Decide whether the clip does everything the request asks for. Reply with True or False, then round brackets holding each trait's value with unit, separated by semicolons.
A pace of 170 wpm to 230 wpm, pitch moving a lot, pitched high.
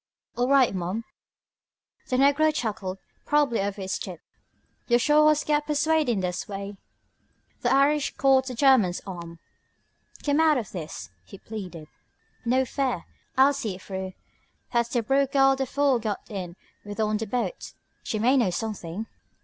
False (155 wpm; 5.8 semitones; 235 Hz)